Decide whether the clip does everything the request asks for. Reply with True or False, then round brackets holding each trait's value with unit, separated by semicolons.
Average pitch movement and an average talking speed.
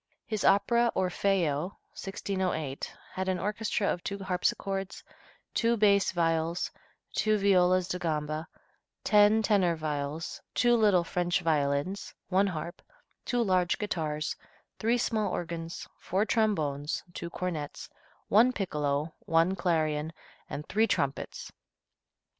False (4.1 semitones; 115 wpm)